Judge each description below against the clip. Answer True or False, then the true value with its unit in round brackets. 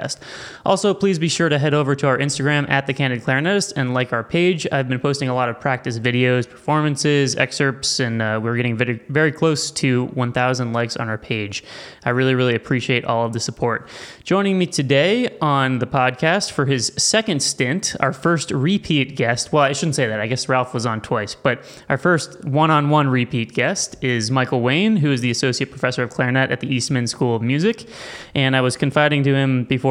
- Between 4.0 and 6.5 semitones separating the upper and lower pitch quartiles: False (3.3 semitones)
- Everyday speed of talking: False (210 wpm)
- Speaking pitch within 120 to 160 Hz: True (135 Hz)